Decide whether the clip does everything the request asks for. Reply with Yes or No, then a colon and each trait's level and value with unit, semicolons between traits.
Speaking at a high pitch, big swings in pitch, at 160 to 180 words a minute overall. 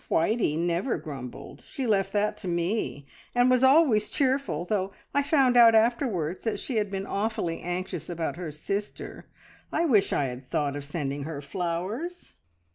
Yes: high, 195 Hz; wide, 6.4 semitones; average, 165 wpm